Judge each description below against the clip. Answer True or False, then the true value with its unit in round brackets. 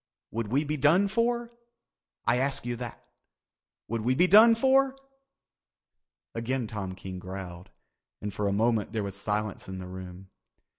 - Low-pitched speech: True (115 Hz)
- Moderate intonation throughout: False (7.7 semitones)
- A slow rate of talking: False (155 wpm)